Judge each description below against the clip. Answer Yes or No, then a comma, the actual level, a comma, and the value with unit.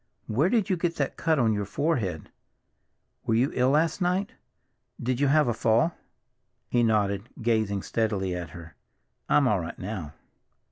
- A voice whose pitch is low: Yes, low, 115 Hz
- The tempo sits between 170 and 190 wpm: No, average, 160 wpm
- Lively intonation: Yes, wide, 7.0 semitones